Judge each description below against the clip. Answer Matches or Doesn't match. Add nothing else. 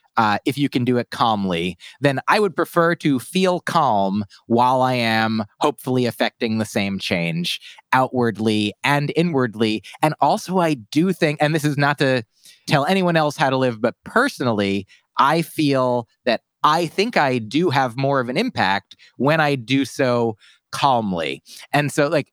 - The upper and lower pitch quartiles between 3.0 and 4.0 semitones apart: Doesn't match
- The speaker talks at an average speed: Matches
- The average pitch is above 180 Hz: Doesn't match